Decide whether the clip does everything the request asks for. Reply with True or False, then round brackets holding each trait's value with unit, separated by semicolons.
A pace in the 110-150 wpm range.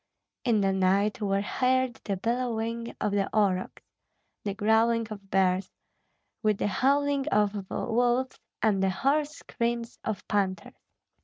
True (135 wpm)